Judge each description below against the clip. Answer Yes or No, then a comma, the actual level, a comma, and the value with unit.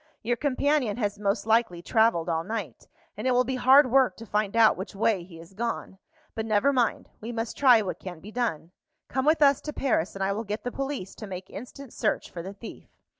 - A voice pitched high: Yes, high, 220 Hz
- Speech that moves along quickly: Yes, fast, 225 wpm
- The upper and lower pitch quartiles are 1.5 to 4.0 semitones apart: No, average, 4.5 semitones